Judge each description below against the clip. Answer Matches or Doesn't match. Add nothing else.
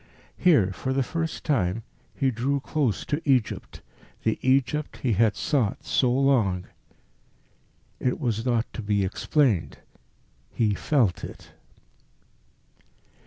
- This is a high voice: Doesn't match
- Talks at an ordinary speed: Doesn't match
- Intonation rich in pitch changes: Doesn't match